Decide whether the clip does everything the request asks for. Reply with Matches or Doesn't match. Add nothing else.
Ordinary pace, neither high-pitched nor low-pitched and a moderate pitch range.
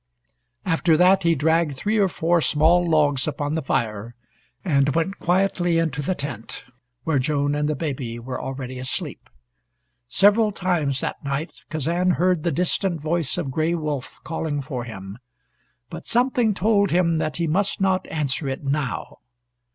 Matches